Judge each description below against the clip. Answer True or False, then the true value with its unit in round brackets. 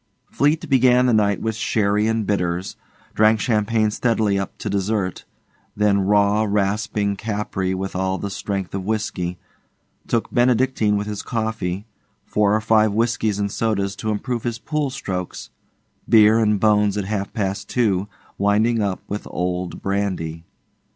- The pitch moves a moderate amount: False (2.2 semitones)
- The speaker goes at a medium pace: True (150 wpm)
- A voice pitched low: True (105 Hz)